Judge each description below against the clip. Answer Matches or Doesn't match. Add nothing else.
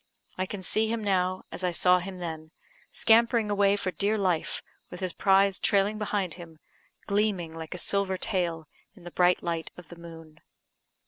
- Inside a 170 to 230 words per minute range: Matches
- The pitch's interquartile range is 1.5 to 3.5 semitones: Matches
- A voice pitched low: Doesn't match